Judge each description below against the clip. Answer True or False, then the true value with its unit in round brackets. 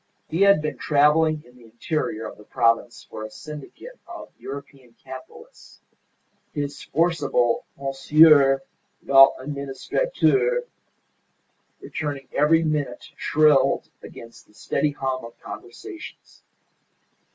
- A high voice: False (140 Hz)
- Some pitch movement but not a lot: True (3.1 semitones)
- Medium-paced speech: False (105 wpm)